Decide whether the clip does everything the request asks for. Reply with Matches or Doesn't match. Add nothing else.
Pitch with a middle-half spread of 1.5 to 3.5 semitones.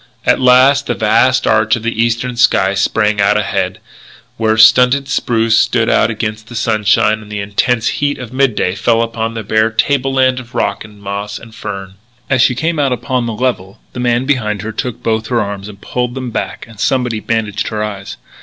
Matches